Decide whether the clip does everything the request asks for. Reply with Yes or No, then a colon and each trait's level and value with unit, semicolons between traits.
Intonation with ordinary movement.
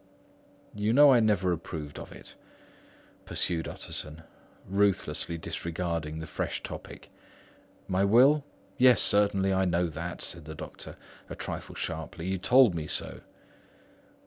Yes: average, 3.9 semitones